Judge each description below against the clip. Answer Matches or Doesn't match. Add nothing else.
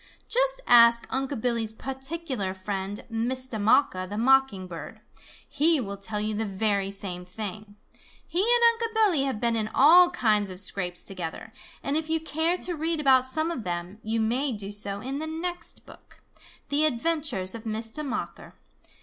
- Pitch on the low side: Doesn't match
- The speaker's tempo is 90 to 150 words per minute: Doesn't match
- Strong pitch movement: Matches